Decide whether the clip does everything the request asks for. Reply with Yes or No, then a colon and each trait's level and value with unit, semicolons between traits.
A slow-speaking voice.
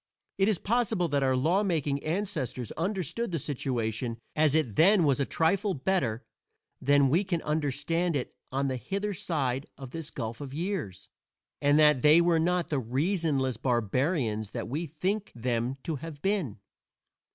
No: average, 165 wpm